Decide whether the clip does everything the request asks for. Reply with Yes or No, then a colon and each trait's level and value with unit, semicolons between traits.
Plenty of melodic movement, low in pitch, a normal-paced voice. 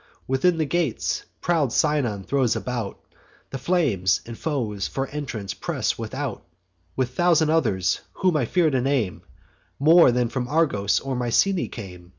Yes: wide, 5.8 semitones; low, 130 Hz; average, 150 wpm